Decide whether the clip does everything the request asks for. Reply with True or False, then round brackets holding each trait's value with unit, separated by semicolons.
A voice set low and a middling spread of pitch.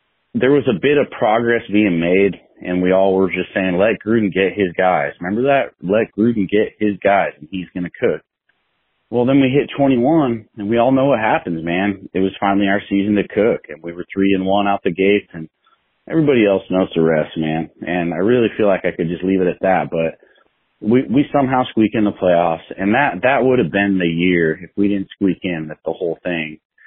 True (95 Hz; 3.4 semitones)